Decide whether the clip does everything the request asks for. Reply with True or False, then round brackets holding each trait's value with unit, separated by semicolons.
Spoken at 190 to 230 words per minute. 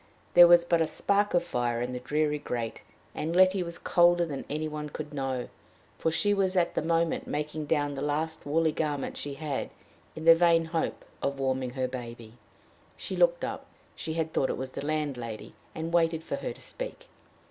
True (200 wpm)